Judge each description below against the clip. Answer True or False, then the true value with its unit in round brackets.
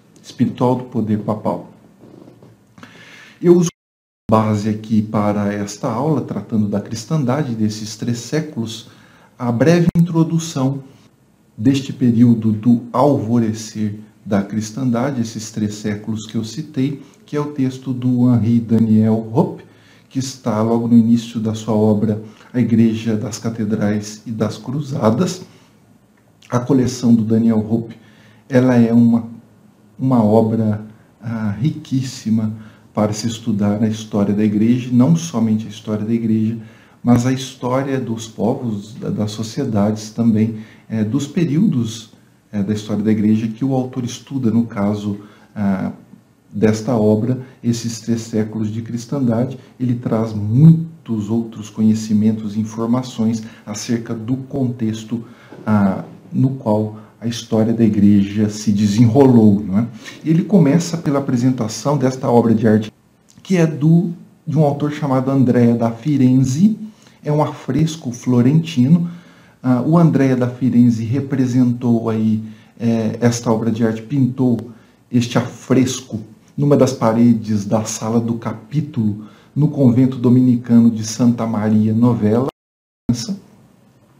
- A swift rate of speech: False (130 wpm)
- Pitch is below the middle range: True (115 Hz)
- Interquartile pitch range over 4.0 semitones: False (3.1 semitones)